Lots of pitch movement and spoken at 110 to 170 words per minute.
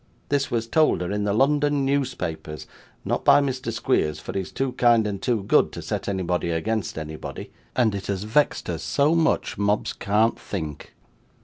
No: wide, 6.1 semitones; average, 185 wpm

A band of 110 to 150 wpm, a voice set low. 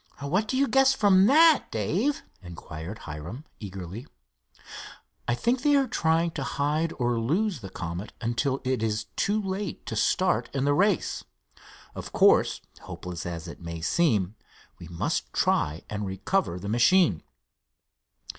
Yes: average, 145 wpm; low, 130 Hz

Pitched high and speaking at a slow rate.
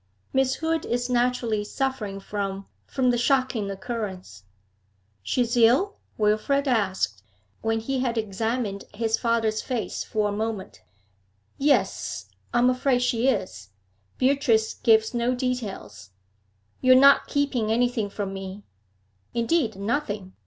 Yes: high, 230 Hz; slow, 130 wpm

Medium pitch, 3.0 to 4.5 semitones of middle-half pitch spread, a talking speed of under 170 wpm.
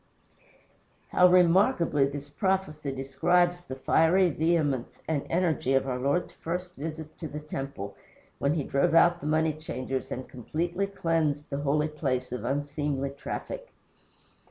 Yes: medium, 150 Hz; average, 3.8 semitones; average, 140 wpm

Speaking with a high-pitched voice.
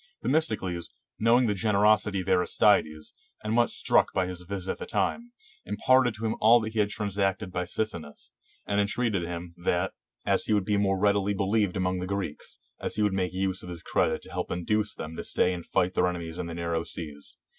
No: very low, 95 Hz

